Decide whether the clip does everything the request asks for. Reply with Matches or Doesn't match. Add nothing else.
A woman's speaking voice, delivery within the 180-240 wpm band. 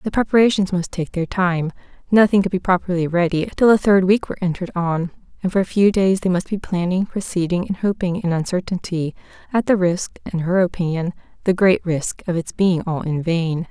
Matches